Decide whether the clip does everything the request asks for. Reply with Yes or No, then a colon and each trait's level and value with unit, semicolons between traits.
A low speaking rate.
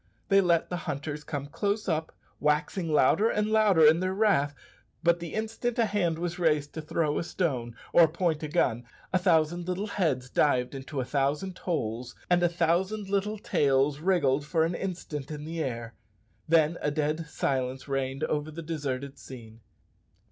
No: average, 175 wpm